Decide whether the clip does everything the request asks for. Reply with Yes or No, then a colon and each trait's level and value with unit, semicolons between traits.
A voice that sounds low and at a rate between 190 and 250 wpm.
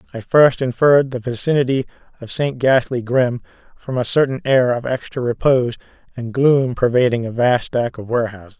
No: low, 125 Hz; average, 170 wpm